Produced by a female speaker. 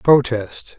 No: male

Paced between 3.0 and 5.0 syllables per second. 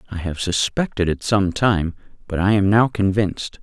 Yes: 4.9 syllables/s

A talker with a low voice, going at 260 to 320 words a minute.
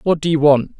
No: medium, 155 Hz; fast, 300 wpm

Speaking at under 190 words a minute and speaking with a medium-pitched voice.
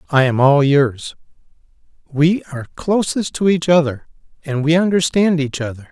Yes: average, 150 wpm; medium, 155 Hz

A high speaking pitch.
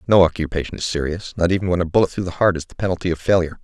No: very low, 85 Hz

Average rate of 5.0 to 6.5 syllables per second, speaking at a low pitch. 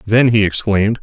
Yes: 5.6 syllables/s; low, 105 Hz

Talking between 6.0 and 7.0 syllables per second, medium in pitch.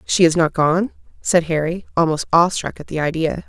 No: 5.2 syllables/s; medium, 165 Hz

